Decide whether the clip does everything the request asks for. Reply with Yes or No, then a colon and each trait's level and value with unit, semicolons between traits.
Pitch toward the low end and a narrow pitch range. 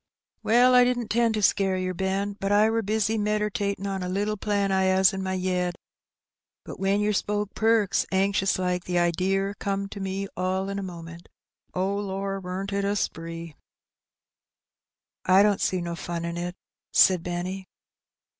No: high, 195 Hz; narrow, 1.9 semitones